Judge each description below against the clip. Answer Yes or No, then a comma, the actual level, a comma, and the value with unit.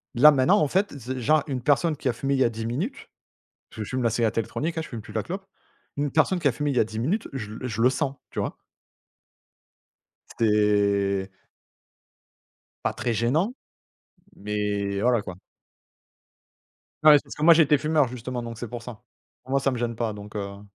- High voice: No, low, 125 Hz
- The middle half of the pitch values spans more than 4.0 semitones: Yes, average, 5.2 semitones